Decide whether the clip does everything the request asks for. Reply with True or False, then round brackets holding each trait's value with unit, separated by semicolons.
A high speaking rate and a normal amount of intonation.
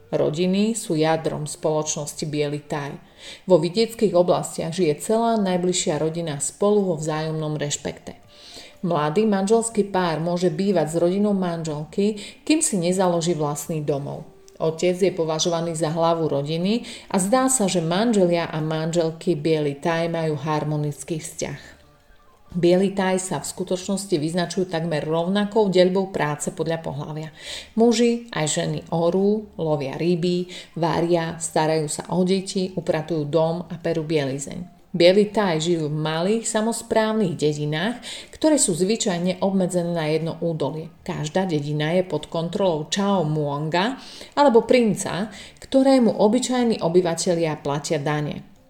False (125 wpm; 3.6 semitones)